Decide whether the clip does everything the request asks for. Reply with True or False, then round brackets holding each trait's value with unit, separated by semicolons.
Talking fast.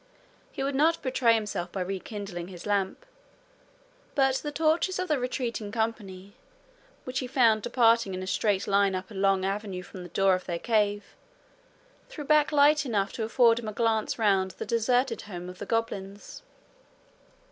False (170 wpm)